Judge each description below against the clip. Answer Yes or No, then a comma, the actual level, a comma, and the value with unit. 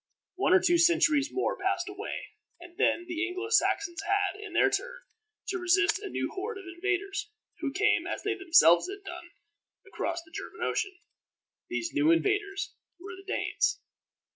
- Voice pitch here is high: Yes, very high, 380 Hz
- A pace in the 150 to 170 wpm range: Yes, average, 165 wpm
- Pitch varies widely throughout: No, average, 2.7 semitones